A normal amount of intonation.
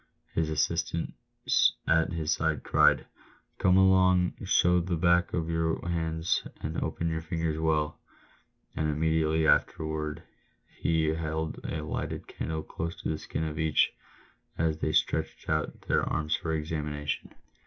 No: narrow, 1.1 semitones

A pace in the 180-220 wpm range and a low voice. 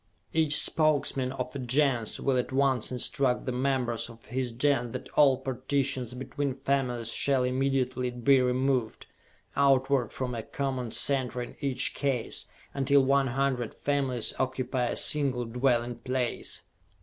No: average, 140 wpm; low, 130 Hz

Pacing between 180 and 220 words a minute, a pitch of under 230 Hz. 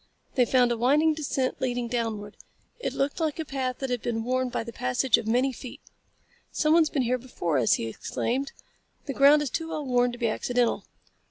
No: average, 200 wpm; very high, 255 Hz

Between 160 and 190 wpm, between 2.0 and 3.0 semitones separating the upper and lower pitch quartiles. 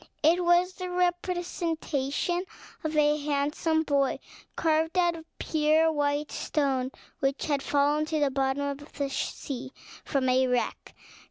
No: average, 140 wpm; average, 2.7 semitones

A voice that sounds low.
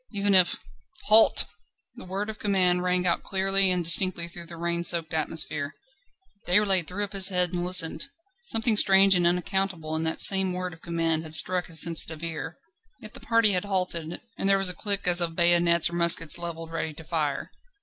No: medium, 175 Hz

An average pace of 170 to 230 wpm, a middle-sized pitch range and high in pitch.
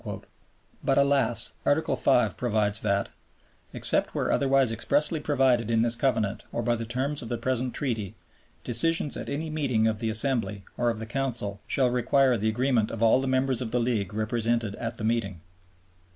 No: average, 180 wpm; average, 3.3 semitones; low, 120 Hz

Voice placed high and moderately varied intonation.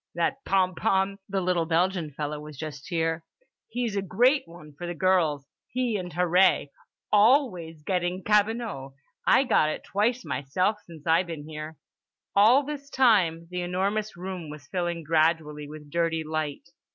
No: medium, 175 Hz; average, 4.2 semitones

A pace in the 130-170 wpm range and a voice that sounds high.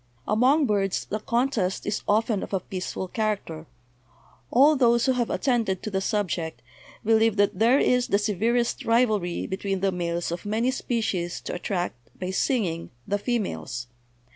Yes: average, 160 wpm; high, 205 Hz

